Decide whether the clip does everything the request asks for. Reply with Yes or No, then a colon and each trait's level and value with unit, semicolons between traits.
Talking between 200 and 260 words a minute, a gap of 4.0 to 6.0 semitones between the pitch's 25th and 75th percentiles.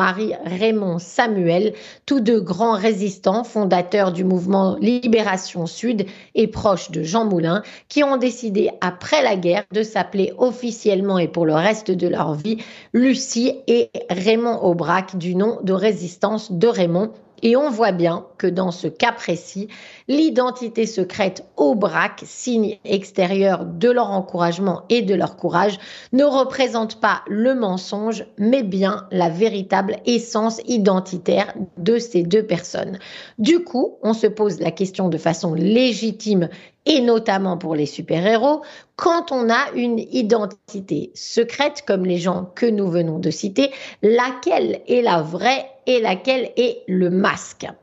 No: average, 150 wpm; average, 4.3 semitones